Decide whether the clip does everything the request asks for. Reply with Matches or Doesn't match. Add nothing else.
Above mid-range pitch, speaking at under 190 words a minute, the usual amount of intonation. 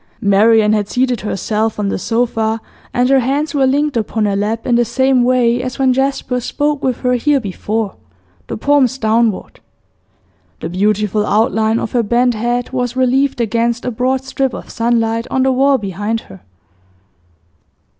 Matches